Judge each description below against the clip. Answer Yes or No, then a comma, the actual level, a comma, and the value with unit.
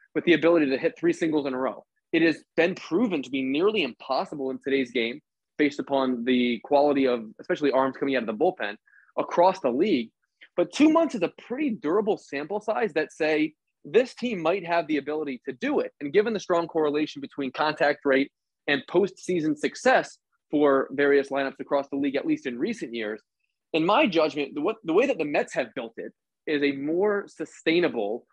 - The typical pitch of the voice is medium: Yes, medium, 155 Hz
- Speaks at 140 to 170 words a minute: No, average, 195 wpm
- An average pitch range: Yes, average, 4.8 semitones